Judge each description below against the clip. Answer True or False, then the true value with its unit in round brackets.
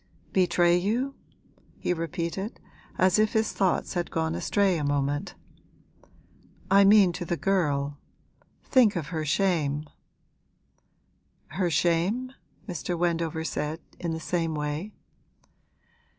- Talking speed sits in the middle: False (115 wpm)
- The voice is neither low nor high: True (175 Hz)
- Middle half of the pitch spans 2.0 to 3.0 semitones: False (3.5 semitones)